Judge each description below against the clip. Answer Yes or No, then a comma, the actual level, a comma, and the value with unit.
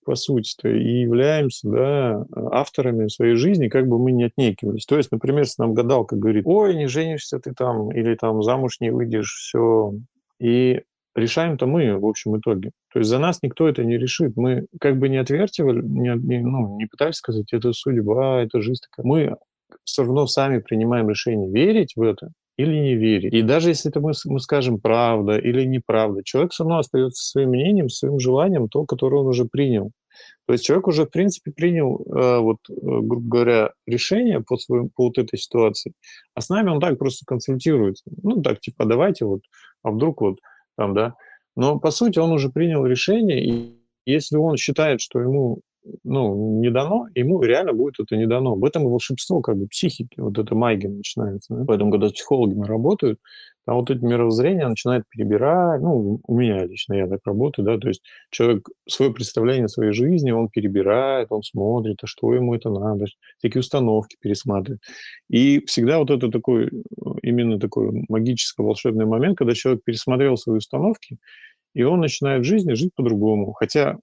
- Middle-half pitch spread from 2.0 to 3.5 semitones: No, average, 4.5 semitones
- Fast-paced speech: Yes, fast, 185 wpm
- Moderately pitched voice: No, low, 125 Hz